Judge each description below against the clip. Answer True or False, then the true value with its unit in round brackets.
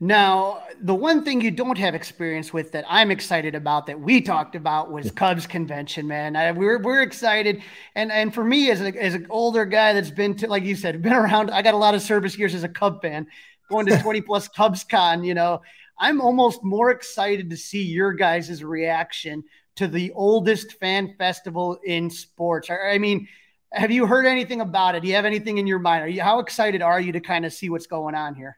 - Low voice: False (195 Hz)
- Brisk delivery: True (225 wpm)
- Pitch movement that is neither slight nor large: True (4.2 semitones)